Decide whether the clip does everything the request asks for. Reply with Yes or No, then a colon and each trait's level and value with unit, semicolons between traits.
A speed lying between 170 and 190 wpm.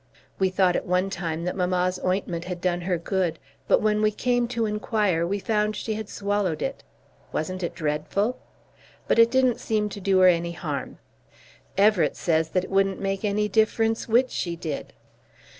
Yes: average, 180 wpm